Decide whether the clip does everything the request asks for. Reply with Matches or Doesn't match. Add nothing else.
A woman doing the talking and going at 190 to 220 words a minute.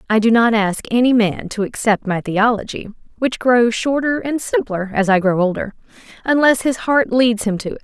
Matches